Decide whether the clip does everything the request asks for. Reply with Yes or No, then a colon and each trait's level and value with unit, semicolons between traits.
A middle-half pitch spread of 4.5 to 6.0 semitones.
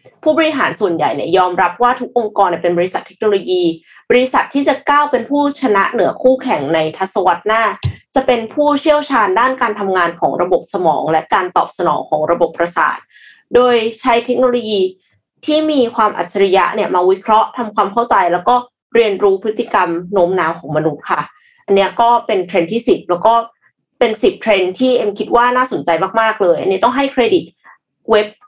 Yes: average, 5.1 semitones